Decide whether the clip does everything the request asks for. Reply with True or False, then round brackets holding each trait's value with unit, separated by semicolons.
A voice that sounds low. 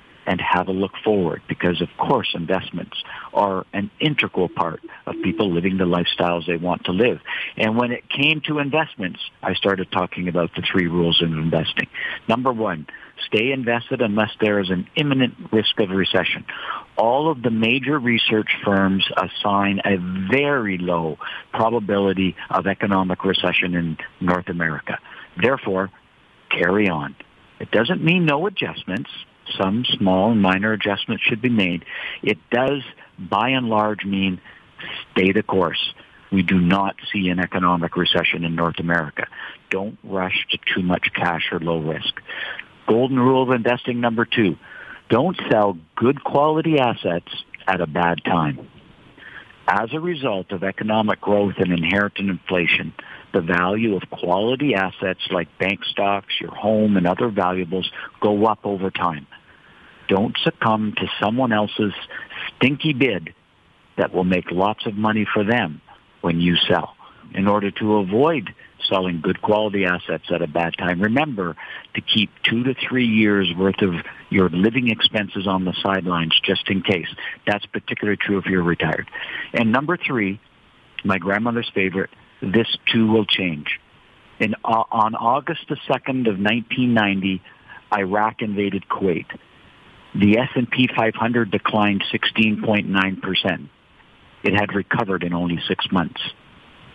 True (100 Hz)